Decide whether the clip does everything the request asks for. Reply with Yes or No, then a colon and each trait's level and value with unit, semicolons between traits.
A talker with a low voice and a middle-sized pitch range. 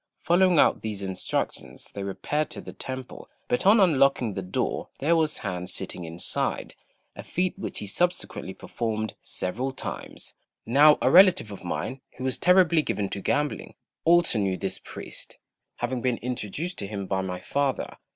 No: low, 125 Hz; wide, 8.2 semitones